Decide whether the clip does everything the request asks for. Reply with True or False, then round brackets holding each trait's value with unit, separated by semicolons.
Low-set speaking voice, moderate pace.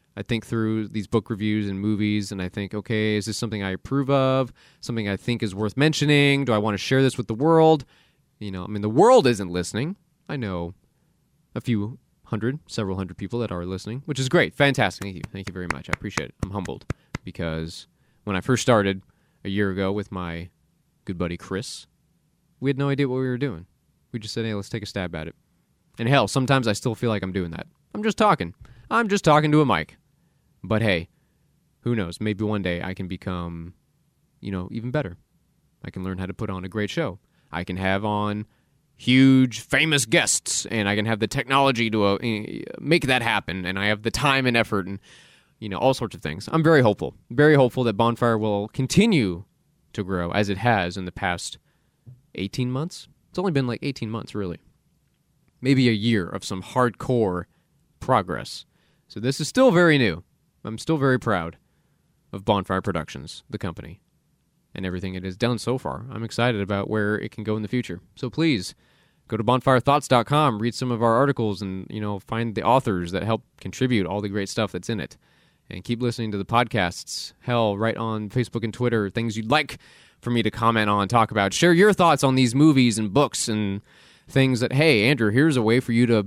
False (110 Hz; 210 wpm)